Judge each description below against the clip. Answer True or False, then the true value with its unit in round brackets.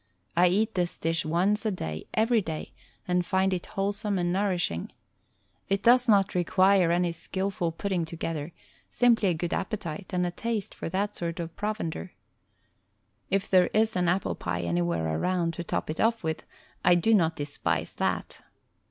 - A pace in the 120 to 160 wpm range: False (170 wpm)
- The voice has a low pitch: False (180 Hz)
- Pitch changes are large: False (3.3 semitones)